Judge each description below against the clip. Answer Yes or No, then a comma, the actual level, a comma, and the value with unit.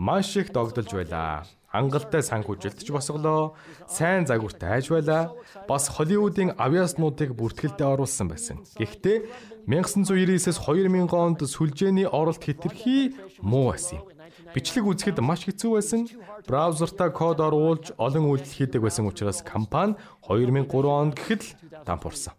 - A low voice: No, medium, 160 Hz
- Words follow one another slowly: Yes, slow, 125 wpm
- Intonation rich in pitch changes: Yes, wide, 5.9 semitones